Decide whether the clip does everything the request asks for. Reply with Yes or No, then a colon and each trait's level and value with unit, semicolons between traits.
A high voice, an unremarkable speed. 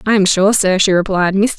No: high, 195 Hz; fast, 265 wpm